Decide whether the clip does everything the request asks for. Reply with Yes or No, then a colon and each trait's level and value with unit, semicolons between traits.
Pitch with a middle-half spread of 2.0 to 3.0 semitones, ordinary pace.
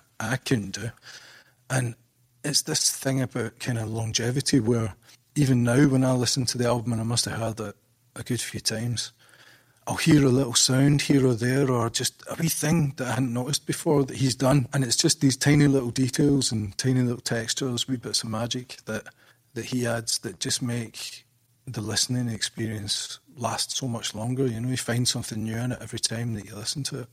No: narrow, 2.4 semitones; fast, 210 wpm